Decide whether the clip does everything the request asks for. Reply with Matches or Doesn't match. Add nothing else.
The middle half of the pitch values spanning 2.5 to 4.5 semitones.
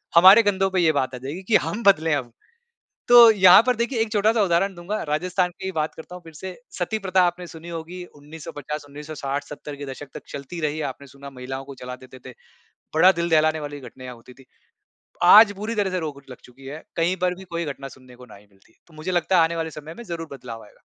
Doesn't match